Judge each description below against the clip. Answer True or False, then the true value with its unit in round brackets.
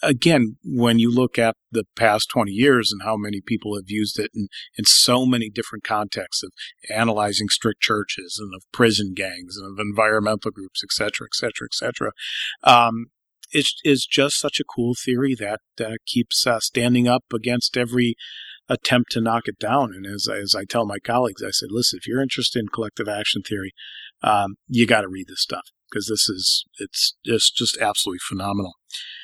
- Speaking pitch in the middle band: False (115 Hz)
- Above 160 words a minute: True (185 wpm)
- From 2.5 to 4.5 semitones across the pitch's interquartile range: True (3.0 semitones)